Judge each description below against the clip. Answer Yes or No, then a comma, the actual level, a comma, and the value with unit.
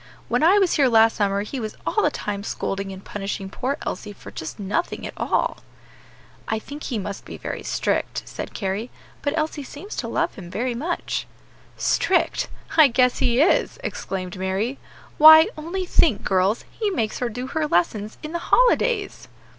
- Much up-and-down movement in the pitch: Yes, wide, 7.6 semitones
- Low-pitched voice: No, high, 240 Hz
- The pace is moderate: Yes, average, 180 wpm